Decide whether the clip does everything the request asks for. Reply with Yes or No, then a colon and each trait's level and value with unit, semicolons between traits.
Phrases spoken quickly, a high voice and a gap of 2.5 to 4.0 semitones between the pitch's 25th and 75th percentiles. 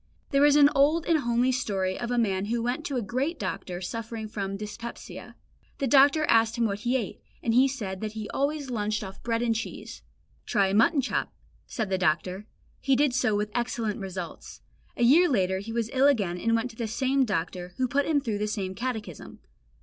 No: fast, 210 wpm; high, 230 Hz; average, 4.5 semitones